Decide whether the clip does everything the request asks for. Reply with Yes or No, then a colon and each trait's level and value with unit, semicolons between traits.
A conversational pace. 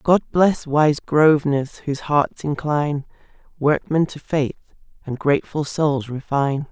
No: slow, 125 wpm